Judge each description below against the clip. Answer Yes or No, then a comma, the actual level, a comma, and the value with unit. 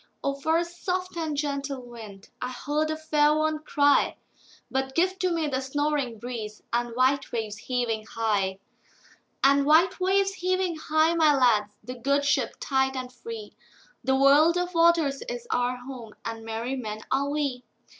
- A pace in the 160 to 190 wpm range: No, average, 145 wpm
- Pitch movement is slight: No, average, 4.3 semitones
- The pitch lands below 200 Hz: No, very high, 280 Hz